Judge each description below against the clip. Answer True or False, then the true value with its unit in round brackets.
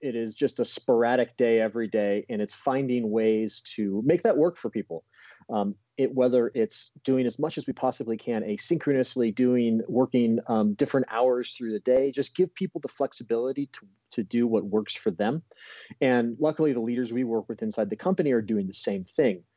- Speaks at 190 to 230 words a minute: True (200 wpm)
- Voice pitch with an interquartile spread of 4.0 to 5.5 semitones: False (3.2 semitones)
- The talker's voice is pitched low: True (120 Hz)